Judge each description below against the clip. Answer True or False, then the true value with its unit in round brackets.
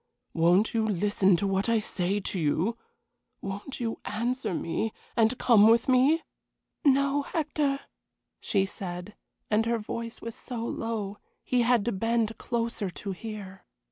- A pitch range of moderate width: True (3.3 semitones)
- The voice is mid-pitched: False (225 Hz)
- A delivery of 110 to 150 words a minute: True (145 wpm)